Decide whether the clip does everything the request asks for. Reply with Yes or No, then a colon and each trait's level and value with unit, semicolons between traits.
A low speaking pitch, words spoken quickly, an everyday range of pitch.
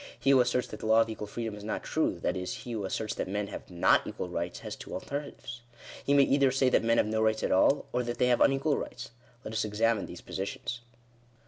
Yes: low, 115 Hz; fast, 250 wpm; average, 3.2 semitones